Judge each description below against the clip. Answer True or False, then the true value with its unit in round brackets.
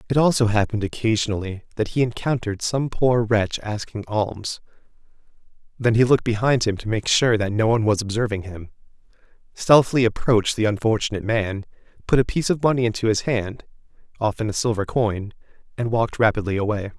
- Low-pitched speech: True (110 Hz)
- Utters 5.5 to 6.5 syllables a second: True (6.1 syllables/s)